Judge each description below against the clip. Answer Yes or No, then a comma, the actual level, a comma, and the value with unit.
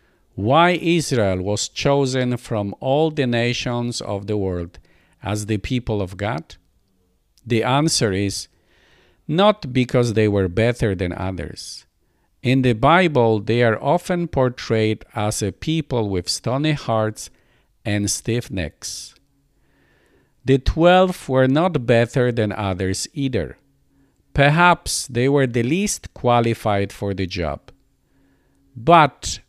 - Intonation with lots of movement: Yes, wide, 5.7 semitones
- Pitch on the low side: Yes, low, 115 Hz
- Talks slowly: Yes, slow, 120 wpm